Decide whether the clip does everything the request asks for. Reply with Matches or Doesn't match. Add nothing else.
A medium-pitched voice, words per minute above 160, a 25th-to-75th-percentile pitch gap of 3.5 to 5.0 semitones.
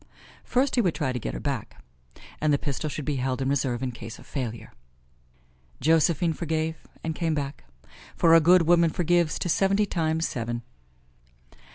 Matches